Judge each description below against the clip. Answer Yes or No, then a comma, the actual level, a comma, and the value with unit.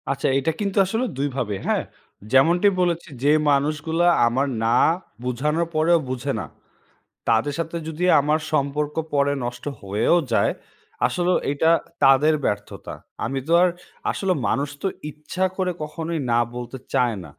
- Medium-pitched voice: Yes, medium, 150 Hz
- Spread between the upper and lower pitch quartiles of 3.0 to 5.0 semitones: Yes, average, 4.2 semitones